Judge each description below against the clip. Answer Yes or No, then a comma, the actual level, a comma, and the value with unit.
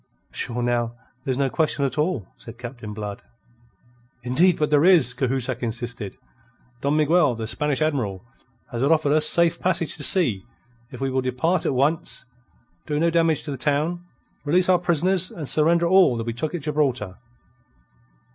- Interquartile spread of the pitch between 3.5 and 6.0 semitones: Yes, average, 5.1 semitones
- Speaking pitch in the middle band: Yes, medium, 145 Hz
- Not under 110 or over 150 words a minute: No, average, 165 wpm